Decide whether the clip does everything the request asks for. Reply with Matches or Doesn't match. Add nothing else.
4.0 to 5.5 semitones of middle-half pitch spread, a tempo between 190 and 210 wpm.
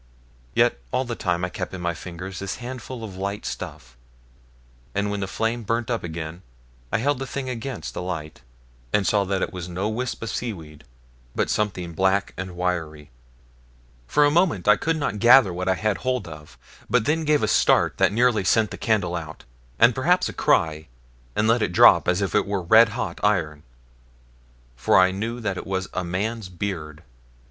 Matches